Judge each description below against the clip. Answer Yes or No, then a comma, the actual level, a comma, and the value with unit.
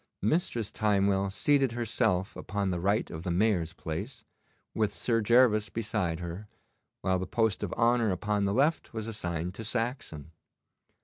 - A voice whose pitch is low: Yes, low, 105 Hz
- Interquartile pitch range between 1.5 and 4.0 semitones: Yes, average, 3.7 semitones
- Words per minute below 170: Yes, average, 150 wpm